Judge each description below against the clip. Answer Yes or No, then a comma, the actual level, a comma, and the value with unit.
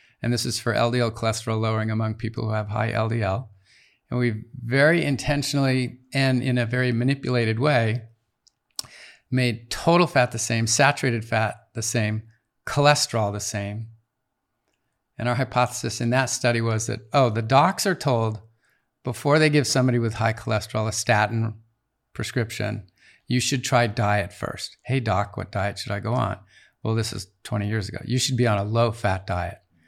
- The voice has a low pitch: Yes, low, 115 Hz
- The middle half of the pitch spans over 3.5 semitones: No, narrow, 2.5 semitones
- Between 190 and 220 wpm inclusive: No, average, 170 wpm